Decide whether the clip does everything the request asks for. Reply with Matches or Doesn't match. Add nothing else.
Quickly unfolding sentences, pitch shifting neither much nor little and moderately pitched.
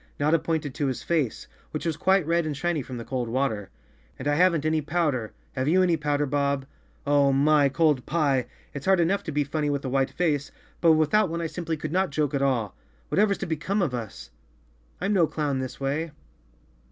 Matches